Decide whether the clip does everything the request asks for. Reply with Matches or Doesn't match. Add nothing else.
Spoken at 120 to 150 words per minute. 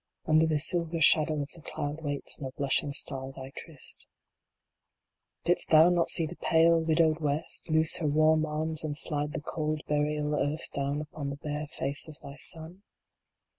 Doesn't match